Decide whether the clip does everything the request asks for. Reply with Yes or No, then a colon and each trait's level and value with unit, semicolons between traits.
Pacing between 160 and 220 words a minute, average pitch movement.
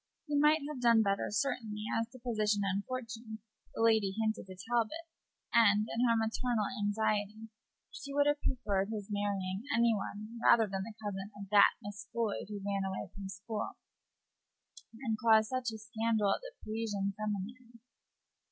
No: average, 165 wpm; narrow, 2.3 semitones